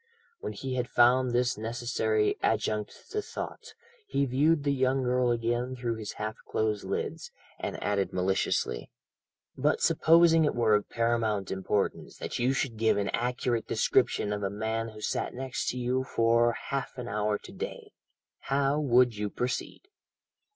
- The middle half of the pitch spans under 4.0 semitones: Yes, average, 3.1 semitones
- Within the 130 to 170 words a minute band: Yes, average, 160 wpm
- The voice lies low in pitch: Yes, low, 120 Hz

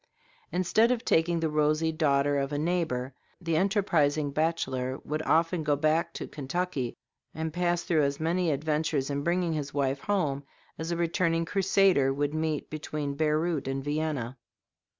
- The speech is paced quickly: No, average, 155 wpm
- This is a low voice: No, medium, 155 Hz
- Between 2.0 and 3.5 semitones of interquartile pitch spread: Yes, average, 3.0 semitones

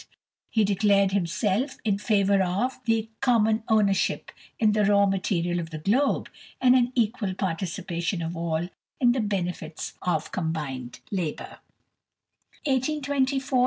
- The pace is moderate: No, slow, 125 wpm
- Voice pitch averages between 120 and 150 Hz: No, high, 195 Hz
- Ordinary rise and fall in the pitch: Yes, average, 4.0 semitones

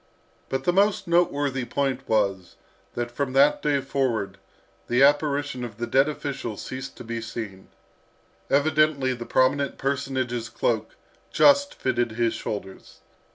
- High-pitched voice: No, low, 130 Hz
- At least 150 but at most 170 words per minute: No, slow, 135 wpm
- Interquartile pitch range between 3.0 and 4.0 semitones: Yes, average, 3.3 semitones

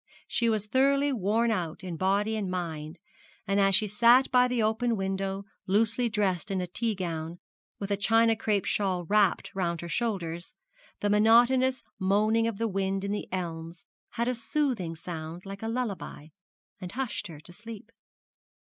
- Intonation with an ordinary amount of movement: Yes, average, 3.9 semitones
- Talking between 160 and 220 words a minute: Yes, average, 170 wpm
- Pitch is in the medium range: No, high, 205 Hz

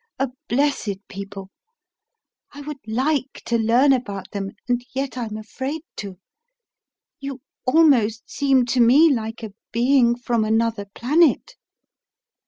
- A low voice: No, high, 245 Hz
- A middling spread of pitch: Yes, average, 3.9 semitones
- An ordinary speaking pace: No, slow, 125 wpm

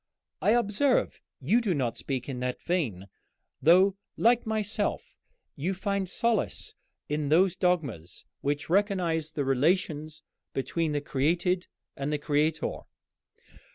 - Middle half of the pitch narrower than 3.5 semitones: No, average, 5.2 semitones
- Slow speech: Yes, slow, 120 wpm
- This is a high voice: No, medium, 165 Hz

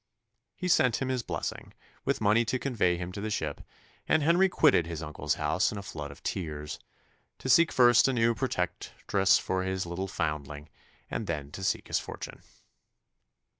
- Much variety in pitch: Yes, wide, 7.2 semitones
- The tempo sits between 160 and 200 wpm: Yes, average, 175 wpm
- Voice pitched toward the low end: Yes, very low, 95 Hz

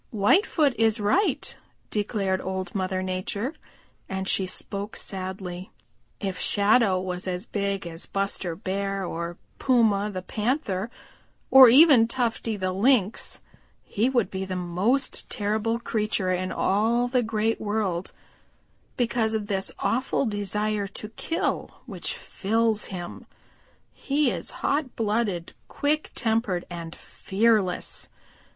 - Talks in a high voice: Yes, high, 205 Hz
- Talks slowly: Yes, slow, 120 wpm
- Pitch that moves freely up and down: No, average, 3.4 semitones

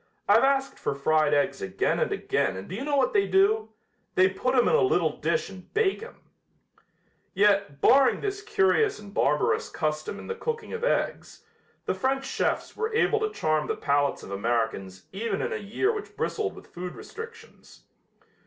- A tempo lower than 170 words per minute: No, average, 185 wpm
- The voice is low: No, high, 210 Hz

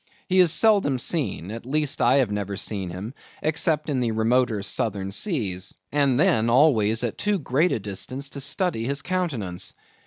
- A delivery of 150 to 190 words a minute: Yes, average, 175 wpm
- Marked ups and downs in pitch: Yes, wide, 6.2 semitones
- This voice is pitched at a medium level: No, low, 125 Hz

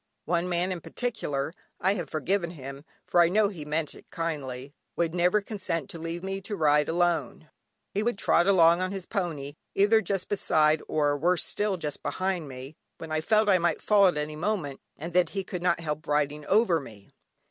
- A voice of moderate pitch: Yes, medium, 170 Hz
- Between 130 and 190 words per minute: No, average, 200 wpm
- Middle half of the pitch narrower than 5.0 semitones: Yes, average, 4.0 semitones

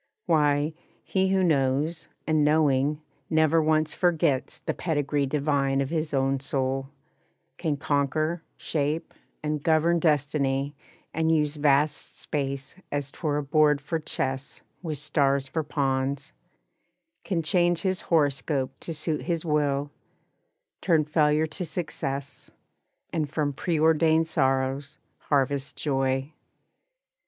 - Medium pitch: Yes, medium, 150 Hz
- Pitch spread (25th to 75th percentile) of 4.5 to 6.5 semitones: No, narrow, 2.4 semitones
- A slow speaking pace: Yes, slow, 120 wpm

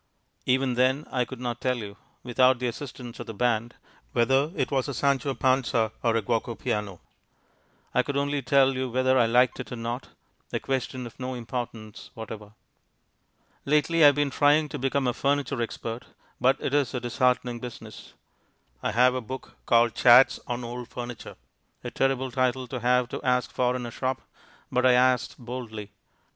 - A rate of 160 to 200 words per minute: Yes, average, 180 wpm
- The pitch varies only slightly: Yes, narrow, 1.9 semitones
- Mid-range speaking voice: No, low, 125 Hz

